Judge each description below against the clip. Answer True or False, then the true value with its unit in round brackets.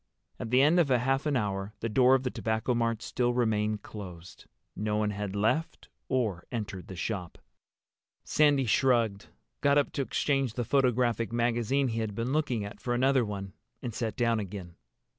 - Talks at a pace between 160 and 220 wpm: True (180 wpm)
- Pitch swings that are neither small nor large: True (3.8 semitones)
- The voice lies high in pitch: False (115 Hz)